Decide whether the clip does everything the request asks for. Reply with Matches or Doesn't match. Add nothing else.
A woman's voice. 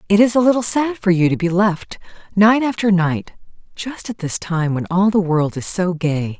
Matches